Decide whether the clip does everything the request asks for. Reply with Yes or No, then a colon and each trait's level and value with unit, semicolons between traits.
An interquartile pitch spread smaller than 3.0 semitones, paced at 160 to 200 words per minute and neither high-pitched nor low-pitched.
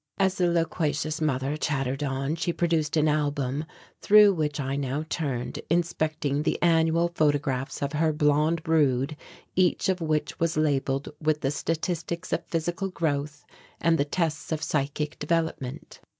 No: narrow, 2.6 semitones; average, 150 wpm; medium, 155 Hz